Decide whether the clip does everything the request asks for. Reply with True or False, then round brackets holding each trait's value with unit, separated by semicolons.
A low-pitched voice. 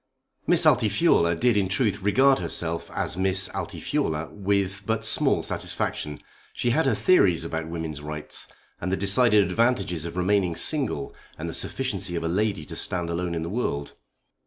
True (95 Hz)